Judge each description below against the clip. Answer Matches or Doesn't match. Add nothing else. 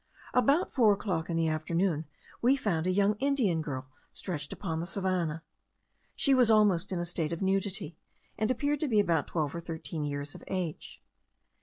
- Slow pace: Doesn't match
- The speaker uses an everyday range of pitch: Matches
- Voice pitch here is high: Doesn't match